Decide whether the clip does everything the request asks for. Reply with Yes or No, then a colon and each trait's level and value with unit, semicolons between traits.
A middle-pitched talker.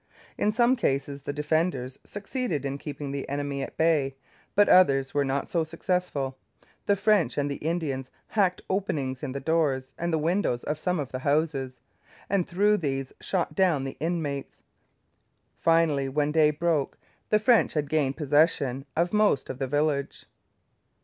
Yes: medium, 150 Hz